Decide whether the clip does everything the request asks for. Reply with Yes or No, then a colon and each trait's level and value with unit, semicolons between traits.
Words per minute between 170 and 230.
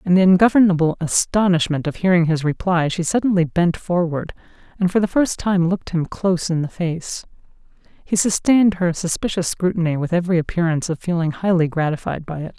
Yes: average, 175 wpm